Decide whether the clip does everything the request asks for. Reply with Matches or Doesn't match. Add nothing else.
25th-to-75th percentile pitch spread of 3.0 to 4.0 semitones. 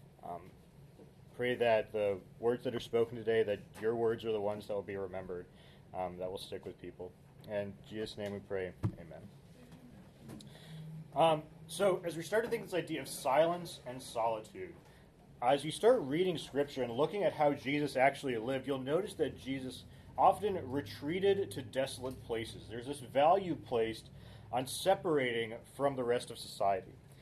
Doesn't match